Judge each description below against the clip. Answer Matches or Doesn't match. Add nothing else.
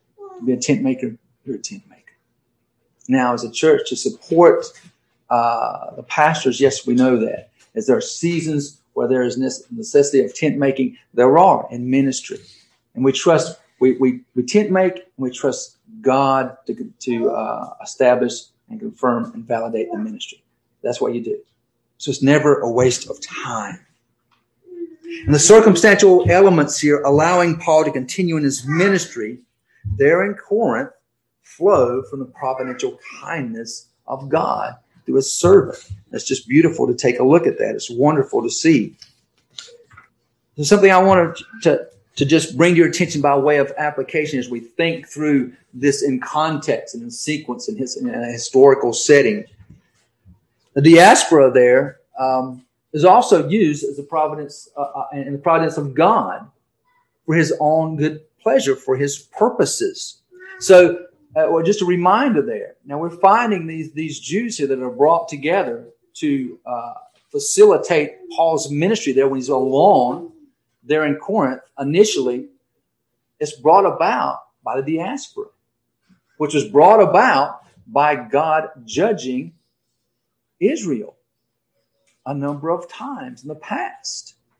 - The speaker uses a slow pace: Doesn't match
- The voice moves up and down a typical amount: Doesn't match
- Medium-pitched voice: Matches